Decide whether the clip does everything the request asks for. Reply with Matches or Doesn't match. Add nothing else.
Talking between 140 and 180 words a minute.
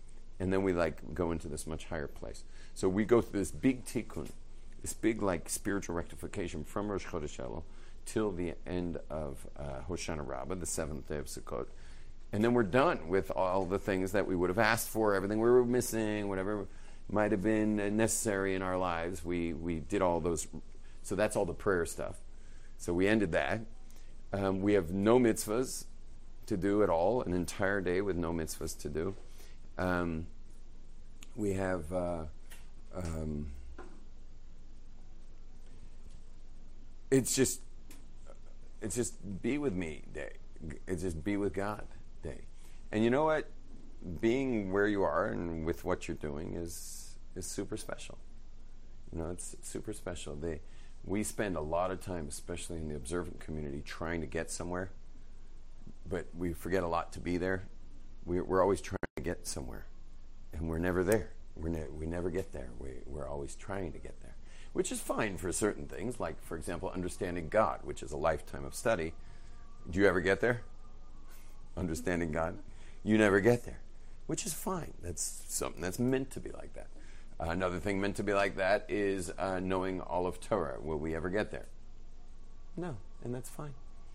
Matches